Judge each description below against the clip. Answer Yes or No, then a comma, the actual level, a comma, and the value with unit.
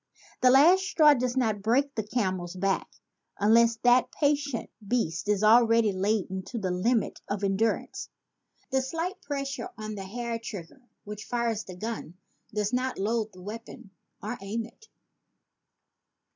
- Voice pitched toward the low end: No, high, 225 Hz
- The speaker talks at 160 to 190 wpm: No, average, 145 wpm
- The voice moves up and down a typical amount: Yes, average, 3.8 semitones